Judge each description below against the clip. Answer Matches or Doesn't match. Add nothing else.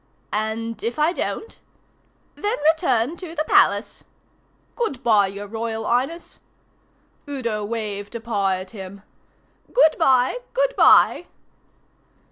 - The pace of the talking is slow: Matches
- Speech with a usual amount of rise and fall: Doesn't match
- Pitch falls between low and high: Doesn't match